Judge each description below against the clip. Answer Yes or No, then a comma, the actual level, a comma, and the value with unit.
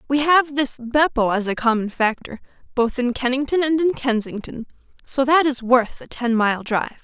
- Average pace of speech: Yes, average, 190 wpm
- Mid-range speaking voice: No, very high, 255 Hz